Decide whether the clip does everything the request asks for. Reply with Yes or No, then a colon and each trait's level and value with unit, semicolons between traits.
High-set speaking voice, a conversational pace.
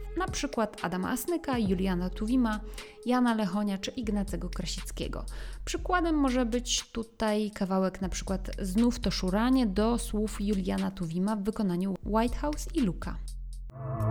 Yes: high, 215 Hz; average, 130 wpm